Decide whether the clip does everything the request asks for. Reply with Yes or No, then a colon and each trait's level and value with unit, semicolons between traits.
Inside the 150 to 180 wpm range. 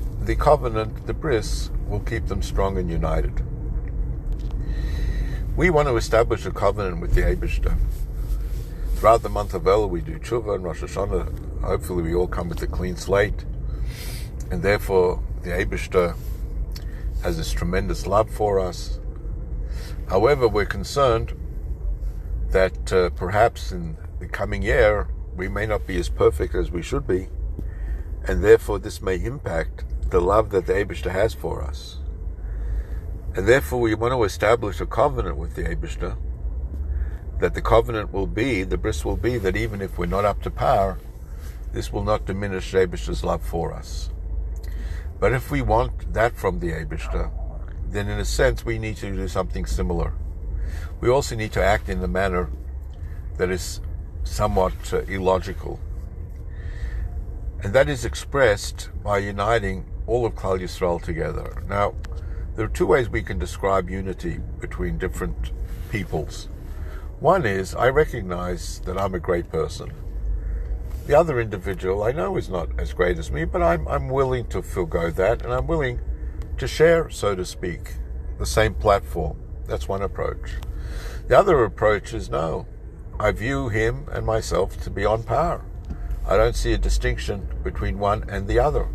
Yes: average, 160 wpm